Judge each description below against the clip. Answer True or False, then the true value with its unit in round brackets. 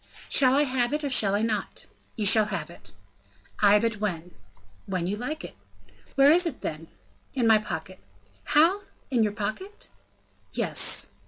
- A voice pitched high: True (220 Hz)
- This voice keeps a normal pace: True (160 wpm)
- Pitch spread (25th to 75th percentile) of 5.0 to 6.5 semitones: True (5.5 semitones)